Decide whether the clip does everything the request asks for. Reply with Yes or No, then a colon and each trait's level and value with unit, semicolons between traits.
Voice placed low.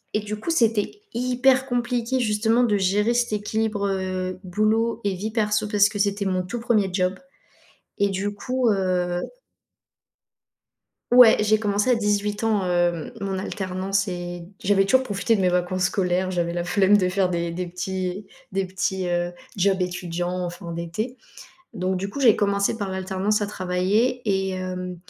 No: high, 195 Hz